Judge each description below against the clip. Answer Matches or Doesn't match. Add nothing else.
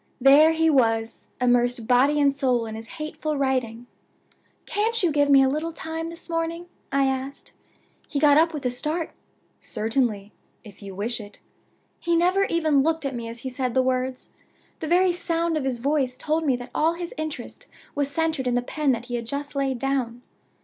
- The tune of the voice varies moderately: Matches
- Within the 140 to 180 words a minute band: Doesn't match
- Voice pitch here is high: Matches